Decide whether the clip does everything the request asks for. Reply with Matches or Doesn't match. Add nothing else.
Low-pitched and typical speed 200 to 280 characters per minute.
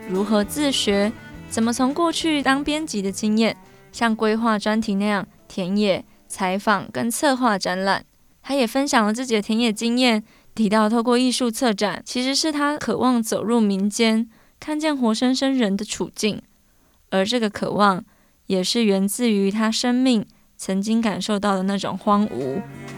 Doesn't match